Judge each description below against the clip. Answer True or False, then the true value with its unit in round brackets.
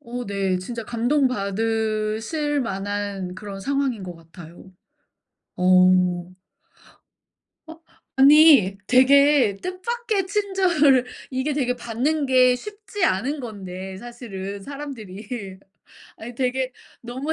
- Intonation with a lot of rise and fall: True (6.3 semitones)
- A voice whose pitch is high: True (240 Hz)